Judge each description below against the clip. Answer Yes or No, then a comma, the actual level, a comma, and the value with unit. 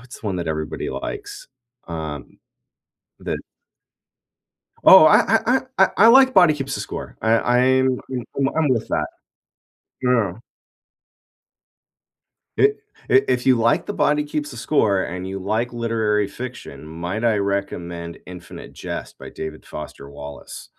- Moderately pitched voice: No, low, 115 Hz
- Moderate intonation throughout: No, wide, 7.6 semitones